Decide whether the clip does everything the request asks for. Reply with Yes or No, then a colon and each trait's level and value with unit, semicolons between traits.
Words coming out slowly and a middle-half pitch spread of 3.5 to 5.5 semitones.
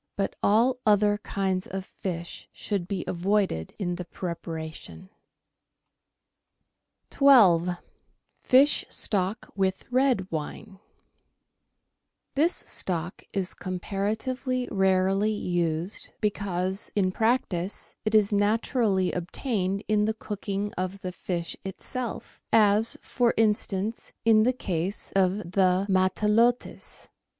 No: slow, 105 wpm; average, 2.9 semitones